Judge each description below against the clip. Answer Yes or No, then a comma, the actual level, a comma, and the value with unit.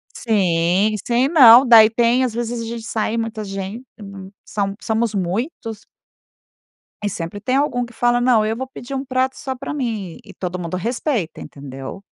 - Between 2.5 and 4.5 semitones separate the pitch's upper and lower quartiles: Yes, average, 3.8 semitones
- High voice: Yes, high, 225 Hz